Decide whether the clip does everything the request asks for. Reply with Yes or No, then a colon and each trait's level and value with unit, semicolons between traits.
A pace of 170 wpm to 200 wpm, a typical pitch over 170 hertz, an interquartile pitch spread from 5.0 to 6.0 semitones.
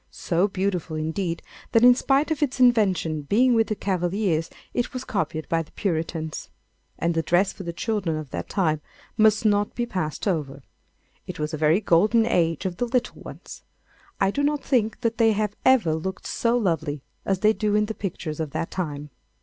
Yes: average, 195 wpm; high, 190 Hz; wide, 5.5 semitones